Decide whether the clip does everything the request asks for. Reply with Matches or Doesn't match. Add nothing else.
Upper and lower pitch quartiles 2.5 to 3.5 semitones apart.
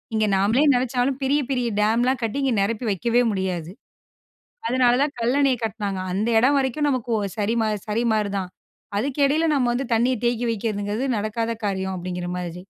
Doesn't match